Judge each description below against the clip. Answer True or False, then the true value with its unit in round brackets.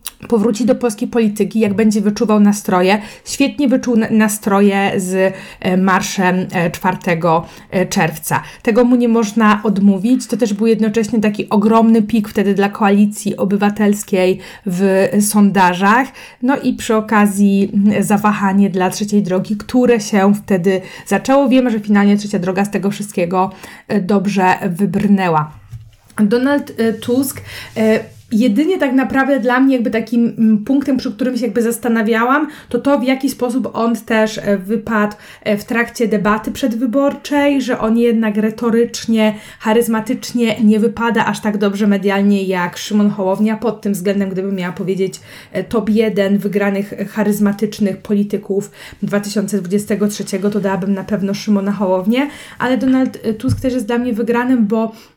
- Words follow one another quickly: False (135 wpm)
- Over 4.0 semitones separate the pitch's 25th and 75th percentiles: False (2.9 semitones)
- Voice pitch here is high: True (210 Hz)